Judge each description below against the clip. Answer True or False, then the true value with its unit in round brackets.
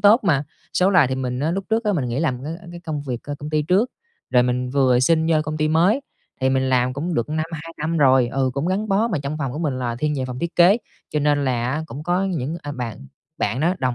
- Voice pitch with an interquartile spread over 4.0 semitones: True (4.7 semitones)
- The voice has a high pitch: False (150 Hz)